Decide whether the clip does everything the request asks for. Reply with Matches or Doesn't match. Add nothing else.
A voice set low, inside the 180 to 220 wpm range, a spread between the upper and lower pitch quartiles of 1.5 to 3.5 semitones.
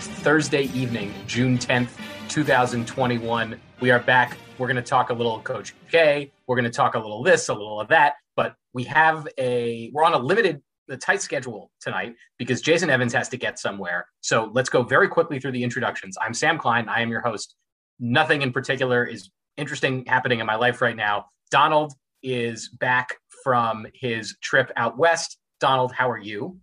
Matches